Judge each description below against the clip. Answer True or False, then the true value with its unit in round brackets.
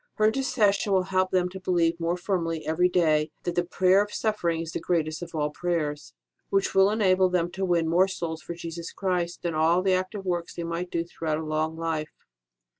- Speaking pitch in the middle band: True (175 Hz)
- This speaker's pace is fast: True (215 wpm)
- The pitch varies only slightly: True (2.2 semitones)